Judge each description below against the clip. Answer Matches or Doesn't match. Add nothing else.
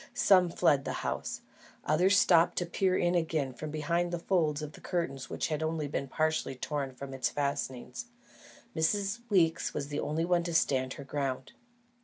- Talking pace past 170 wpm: Matches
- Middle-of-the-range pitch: Matches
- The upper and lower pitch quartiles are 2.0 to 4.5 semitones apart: Matches